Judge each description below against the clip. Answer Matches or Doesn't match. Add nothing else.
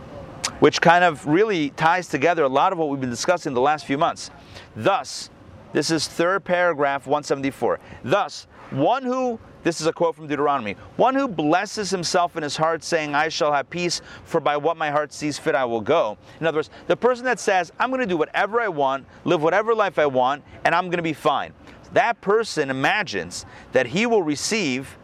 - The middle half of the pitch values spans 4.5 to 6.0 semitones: Doesn't match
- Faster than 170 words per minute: Matches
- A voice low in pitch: Doesn't match